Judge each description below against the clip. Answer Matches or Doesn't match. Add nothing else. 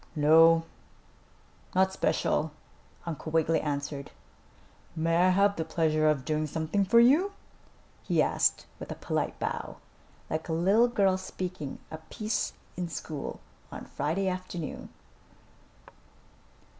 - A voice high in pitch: Doesn't match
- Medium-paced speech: Doesn't match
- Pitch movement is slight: Doesn't match